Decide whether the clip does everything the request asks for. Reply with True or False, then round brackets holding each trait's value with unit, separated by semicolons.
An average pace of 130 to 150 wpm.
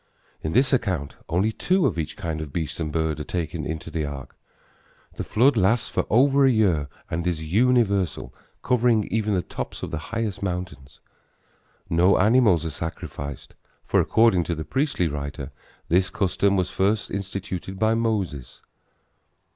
False (160 wpm)